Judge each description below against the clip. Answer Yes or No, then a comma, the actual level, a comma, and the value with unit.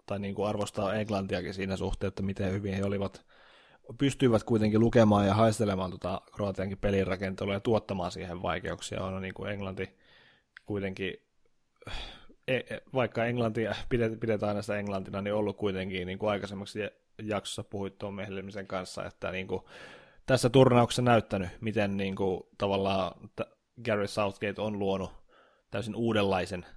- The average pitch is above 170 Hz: No, low, 100 Hz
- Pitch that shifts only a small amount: Yes, narrow, 1.9 semitones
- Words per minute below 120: No, average, 135 wpm